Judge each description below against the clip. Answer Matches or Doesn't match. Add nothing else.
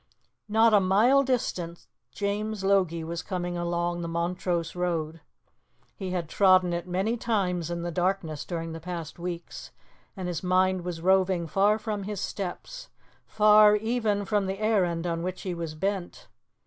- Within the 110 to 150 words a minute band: Doesn't match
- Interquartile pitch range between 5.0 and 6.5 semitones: Doesn't match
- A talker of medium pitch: Matches